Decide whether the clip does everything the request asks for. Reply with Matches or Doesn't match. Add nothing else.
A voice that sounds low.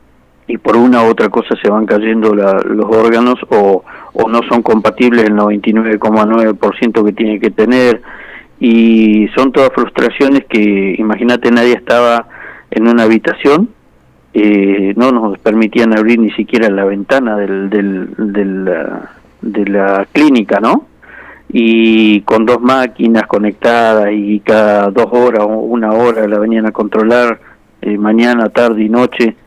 Matches